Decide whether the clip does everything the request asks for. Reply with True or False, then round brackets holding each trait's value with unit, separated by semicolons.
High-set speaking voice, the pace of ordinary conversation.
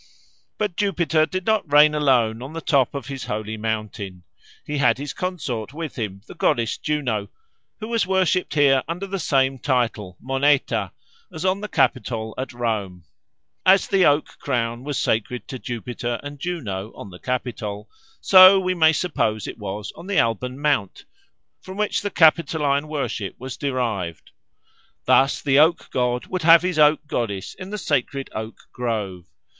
False (135 Hz; 165 wpm)